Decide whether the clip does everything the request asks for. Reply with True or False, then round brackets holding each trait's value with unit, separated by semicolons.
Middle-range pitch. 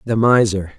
False (110 Hz)